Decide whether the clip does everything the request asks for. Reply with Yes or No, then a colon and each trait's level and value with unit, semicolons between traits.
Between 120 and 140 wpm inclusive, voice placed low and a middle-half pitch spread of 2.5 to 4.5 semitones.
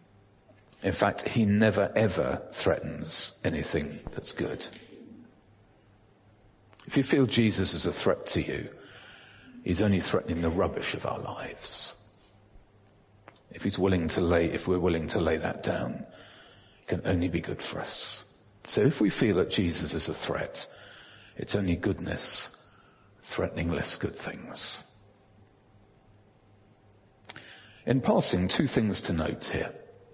Yes: slow, 135 wpm; low, 100 Hz; average, 2.9 semitones